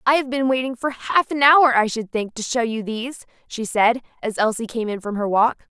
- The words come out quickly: Yes, fast, 250 wpm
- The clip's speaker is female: Yes, female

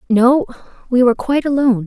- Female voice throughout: Yes, female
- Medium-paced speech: Yes, average, 160 wpm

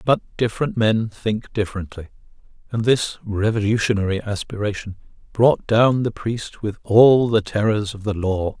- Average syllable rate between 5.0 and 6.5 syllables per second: No, 4.7 syllables/s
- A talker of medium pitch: No, low, 110 Hz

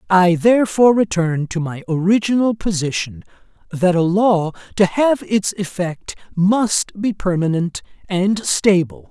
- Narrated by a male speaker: Yes, male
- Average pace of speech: No, slow, 125 wpm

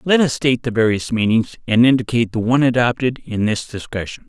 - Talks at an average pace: Yes, average, 195 wpm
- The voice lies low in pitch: Yes, low, 120 Hz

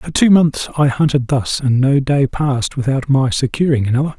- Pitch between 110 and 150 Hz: Yes, low, 135 Hz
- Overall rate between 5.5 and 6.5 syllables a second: No, 5.3 syllables/s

